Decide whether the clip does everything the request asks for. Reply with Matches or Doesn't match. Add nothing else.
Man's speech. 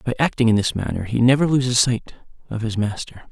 Matches